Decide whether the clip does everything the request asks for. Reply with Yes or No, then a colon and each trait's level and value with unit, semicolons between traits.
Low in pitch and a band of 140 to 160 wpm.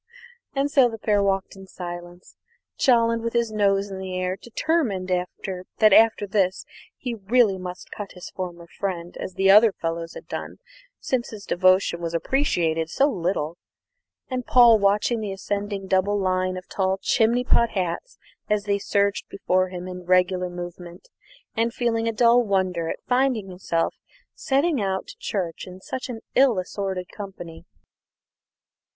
No: high, 195 Hz; average, 155 wpm